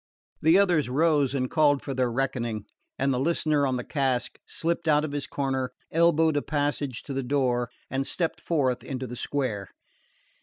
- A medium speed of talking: Yes, average, 180 wpm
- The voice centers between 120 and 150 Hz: Yes, medium, 140 Hz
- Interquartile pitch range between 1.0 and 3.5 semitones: Yes, average, 3.2 semitones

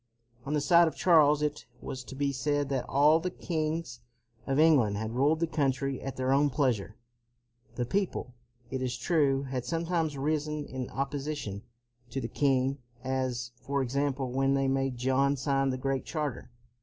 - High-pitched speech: No, low, 135 Hz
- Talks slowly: No, average, 170 wpm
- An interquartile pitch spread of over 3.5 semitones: No, narrow, 2.5 semitones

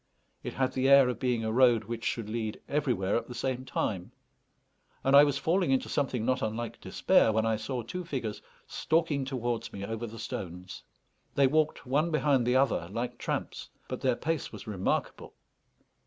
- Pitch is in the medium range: No, low, 125 Hz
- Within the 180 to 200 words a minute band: Yes, average, 185 wpm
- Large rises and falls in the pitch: No, average, 3.7 semitones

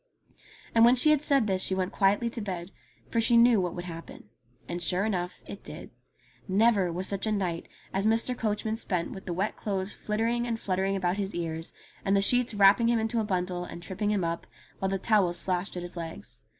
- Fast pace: Yes, fast, 215 wpm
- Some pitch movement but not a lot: Yes, average, 3.7 semitones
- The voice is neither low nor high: No, high, 195 Hz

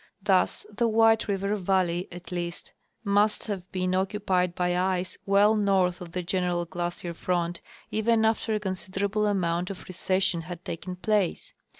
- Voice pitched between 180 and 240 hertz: Yes, medium, 185 Hz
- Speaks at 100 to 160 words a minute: Yes, average, 155 wpm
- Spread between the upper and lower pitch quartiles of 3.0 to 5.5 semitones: No, narrow, 2.4 semitones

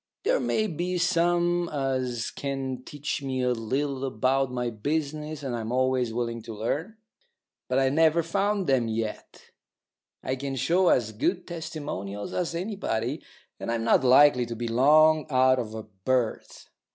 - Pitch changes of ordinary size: Yes, average, 4.9 semitones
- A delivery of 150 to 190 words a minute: Yes, average, 155 wpm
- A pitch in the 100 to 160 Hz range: Yes, low, 135 Hz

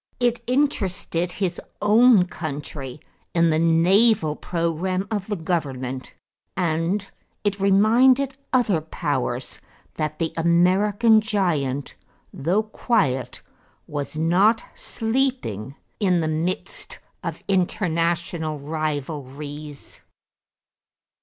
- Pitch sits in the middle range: Yes, medium, 170 Hz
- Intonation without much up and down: No, average, 5.2 semitones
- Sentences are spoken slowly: Yes, slow, 90 wpm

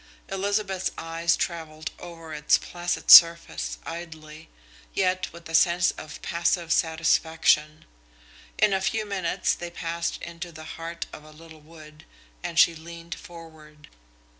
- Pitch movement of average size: No, narrow, 1.6 semitones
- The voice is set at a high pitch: No, medium, 165 Hz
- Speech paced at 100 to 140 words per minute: Yes, slow, 135 wpm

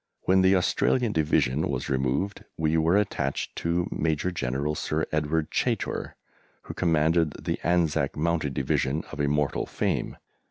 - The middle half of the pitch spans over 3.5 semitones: No, average, 3.0 semitones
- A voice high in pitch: No, very low, 80 Hz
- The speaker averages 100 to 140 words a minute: Yes, slow, 135 wpm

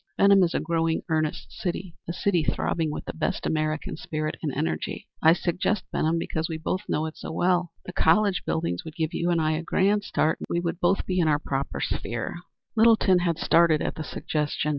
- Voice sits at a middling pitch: Yes, medium, 165 Hz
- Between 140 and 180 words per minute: No, fast, 205 wpm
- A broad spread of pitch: No, narrow, 2.4 semitones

